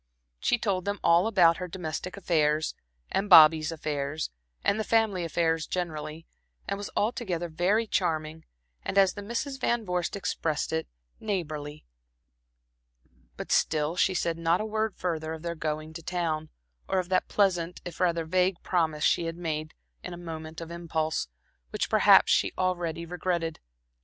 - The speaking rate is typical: Yes, average, 160 wpm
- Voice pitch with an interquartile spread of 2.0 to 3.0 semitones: Yes, average, 2.7 semitones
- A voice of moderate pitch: Yes, medium, 170 Hz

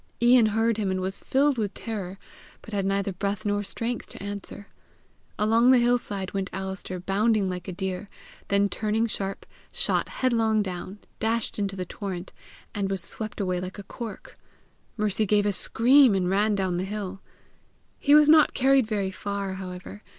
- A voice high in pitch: Yes, high, 205 Hz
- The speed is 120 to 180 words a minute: Yes, average, 170 wpm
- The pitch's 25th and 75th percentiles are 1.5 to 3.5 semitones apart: Yes, average, 2.7 semitones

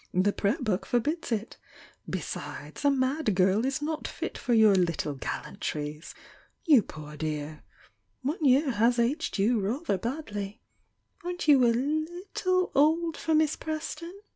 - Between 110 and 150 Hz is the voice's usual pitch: No, very high, 255 Hz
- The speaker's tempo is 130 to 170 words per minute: Yes, average, 140 wpm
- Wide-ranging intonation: Yes, wide, 7.8 semitones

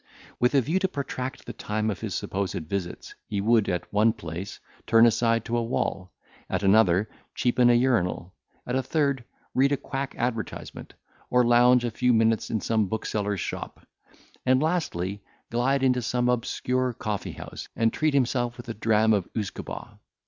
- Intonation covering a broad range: No, average, 3.2 semitones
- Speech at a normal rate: Yes, average, 175 wpm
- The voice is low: Yes, low, 115 Hz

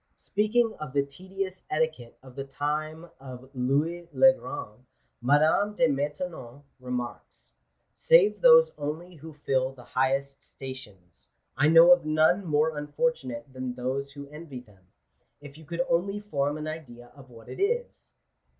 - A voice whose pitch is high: No, medium, 145 Hz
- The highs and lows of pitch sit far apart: No, average, 4.6 semitones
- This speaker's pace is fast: No, average, 155 wpm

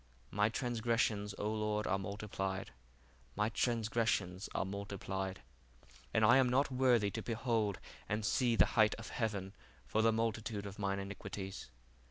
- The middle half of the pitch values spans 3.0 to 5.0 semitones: No, narrow, 2.5 semitones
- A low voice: Yes, low, 105 Hz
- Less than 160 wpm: Yes, average, 145 wpm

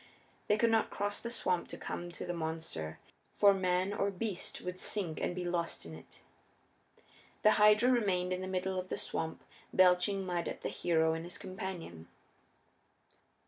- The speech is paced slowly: No, average, 175 wpm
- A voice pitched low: No, medium, 185 Hz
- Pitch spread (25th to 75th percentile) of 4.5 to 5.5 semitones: No, average, 2.7 semitones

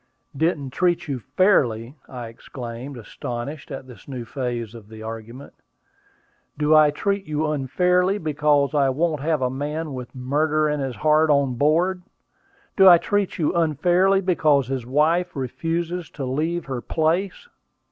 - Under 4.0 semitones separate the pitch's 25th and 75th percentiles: No, average, 4.4 semitones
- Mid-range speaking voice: Yes, medium, 150 Hz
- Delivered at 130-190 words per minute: Yes, average, 150 wpm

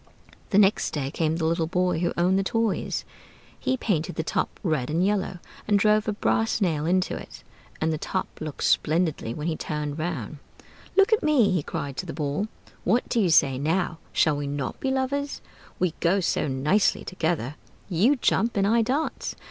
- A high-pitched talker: No, medium, 175 Hz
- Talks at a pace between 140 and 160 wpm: No, average, 190 wpm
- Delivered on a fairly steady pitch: No, average, 5.3 semitones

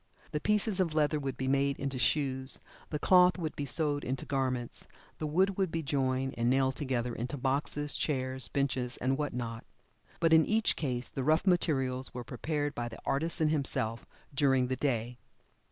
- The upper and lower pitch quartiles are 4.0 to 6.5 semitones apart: No, average, 3.1 semitones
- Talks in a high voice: No, medium, 140 Hz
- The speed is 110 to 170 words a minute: No, average, 180 wpm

